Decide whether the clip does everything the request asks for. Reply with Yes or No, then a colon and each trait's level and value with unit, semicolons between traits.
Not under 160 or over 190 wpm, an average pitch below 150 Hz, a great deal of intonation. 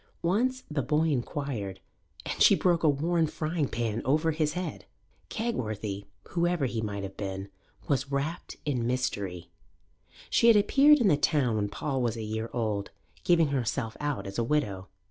Yes: average, 165 wpm; medium, 140 Hz; wide, 6.8 semitones